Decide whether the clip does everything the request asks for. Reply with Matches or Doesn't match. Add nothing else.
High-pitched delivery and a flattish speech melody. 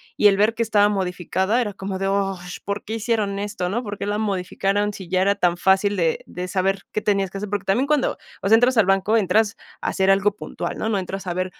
Matches